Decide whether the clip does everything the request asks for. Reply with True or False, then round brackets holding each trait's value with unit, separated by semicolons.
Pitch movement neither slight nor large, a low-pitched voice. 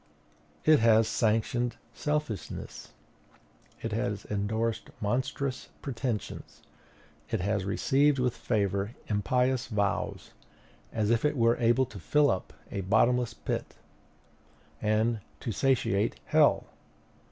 True (3.2 semitones; 115 Hz)